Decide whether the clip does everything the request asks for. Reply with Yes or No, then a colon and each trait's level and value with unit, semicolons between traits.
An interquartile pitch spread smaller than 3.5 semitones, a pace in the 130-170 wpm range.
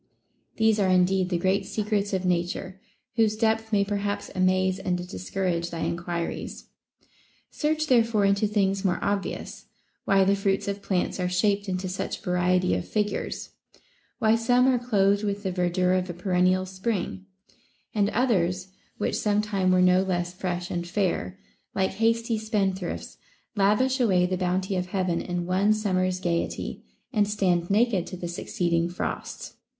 Yes: narrow, 2.4 semitones; average, 160 wpm